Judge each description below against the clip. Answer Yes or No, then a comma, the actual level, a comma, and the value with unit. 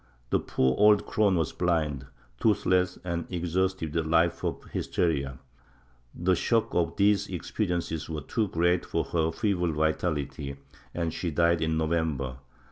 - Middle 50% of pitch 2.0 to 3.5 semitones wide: Yes, narrow, 2.6 semitones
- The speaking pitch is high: No, very low, 85 Hz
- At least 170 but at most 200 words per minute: No, average, 145 wpm